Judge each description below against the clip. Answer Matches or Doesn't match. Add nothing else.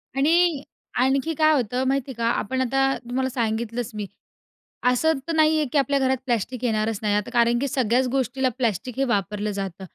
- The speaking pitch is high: Matches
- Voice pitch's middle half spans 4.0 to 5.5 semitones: Doesn't match